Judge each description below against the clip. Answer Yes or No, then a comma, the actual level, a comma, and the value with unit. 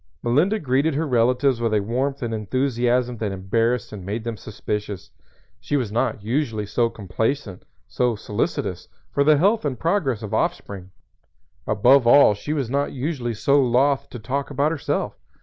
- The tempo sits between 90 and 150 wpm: No, average, 165 wpm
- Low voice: Yes, low, 125 Hz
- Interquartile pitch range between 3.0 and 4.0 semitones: No, average, 4.4 semitones